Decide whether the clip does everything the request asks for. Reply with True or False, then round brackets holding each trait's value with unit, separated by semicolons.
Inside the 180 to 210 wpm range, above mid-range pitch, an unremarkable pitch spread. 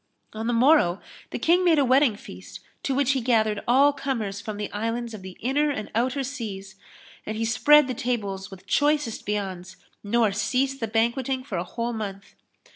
True (190 wpm; 230 Hz; 4.6 semitones)